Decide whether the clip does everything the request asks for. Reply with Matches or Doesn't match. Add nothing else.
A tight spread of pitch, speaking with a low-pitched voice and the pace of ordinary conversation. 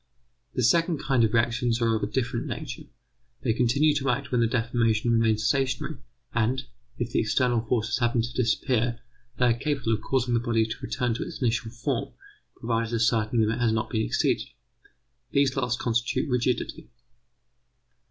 Matches